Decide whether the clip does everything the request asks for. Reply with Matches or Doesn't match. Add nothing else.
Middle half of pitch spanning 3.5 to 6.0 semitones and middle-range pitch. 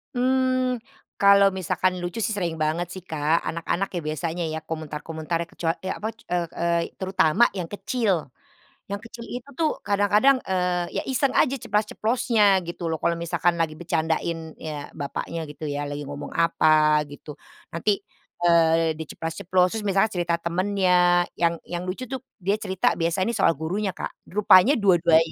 Matches